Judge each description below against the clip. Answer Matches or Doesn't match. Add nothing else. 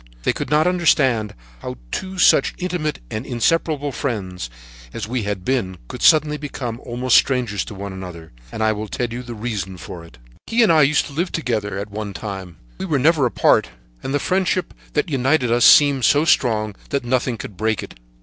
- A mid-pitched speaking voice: Doesn't match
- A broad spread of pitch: Matches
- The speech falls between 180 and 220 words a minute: Matches